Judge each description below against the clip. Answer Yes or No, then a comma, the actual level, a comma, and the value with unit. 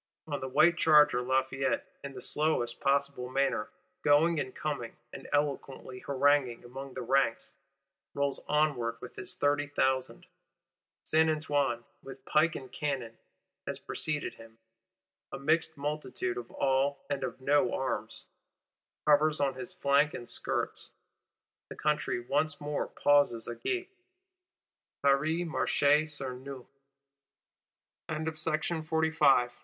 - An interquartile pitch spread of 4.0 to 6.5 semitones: No, narrow, 2.6 semitones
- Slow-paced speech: Yes, slow, 125 wpm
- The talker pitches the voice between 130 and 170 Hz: Yes, medium, 140 Hz